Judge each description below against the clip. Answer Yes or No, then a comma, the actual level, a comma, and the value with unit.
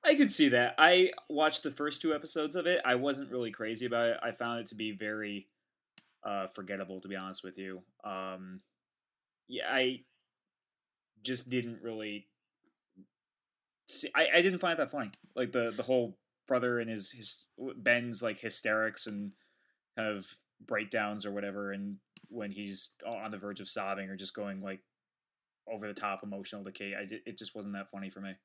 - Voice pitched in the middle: No, low, 110 Hz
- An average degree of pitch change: Yes, average, 4.0 semitones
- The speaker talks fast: No, average, 185 wpm